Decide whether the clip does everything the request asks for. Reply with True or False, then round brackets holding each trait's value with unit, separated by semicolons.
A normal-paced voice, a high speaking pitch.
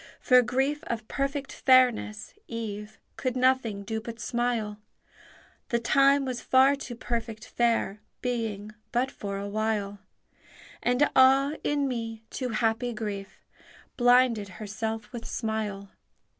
False (125 wpm; 230 Hz)